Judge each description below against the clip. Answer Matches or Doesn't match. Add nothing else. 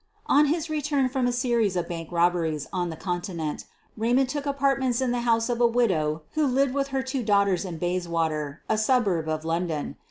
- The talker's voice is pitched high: Matches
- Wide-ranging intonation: Matches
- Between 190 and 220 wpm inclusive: Matches